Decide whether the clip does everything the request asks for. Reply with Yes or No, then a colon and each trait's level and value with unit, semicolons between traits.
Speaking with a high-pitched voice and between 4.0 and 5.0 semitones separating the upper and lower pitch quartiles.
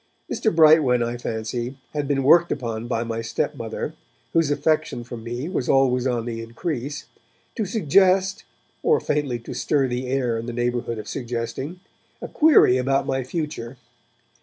No: low, 130 Hz; average, 4.4 semitones